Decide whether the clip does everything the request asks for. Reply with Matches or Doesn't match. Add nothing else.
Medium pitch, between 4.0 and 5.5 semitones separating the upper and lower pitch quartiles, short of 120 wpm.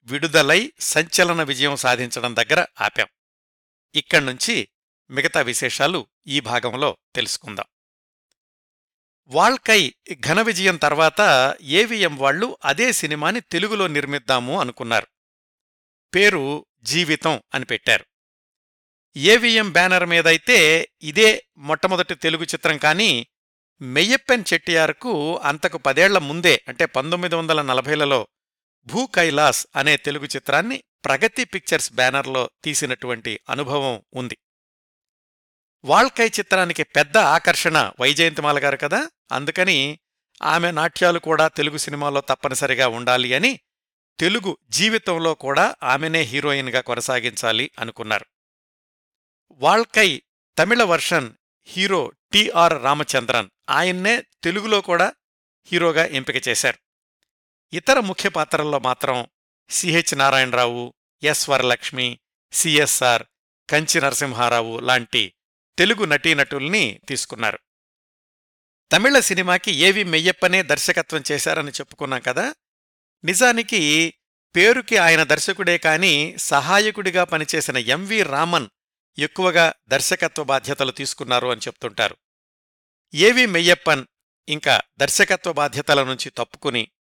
Matches